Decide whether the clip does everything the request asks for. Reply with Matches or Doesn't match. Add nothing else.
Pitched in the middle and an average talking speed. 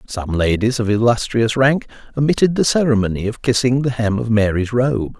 Doesn't match